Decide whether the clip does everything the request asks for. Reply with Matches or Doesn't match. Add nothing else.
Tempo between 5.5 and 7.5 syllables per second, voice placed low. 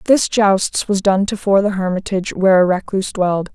Doesn't match